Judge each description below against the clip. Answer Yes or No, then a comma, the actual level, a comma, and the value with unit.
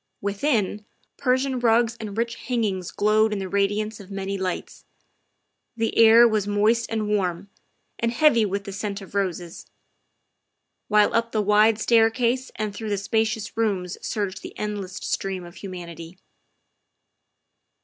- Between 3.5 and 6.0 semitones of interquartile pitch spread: No, narrow, 2.4 semitones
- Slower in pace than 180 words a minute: Yes, average, 140 wpm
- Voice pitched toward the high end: Yes, high, 210 Hz